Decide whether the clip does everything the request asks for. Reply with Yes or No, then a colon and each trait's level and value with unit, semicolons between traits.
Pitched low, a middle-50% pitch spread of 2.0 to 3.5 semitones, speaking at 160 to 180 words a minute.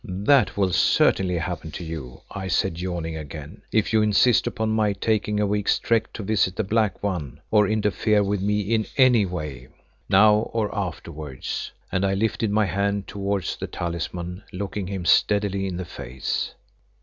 Yes: low, 100 Hz; average, 3.2 semitones; average, 170 wpm